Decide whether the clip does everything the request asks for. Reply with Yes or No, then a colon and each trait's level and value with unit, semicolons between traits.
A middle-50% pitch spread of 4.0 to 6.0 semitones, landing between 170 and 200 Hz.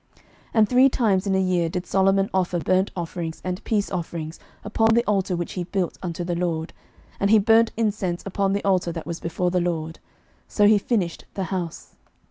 No: average, 2.8 semitones; medium, 185 Hz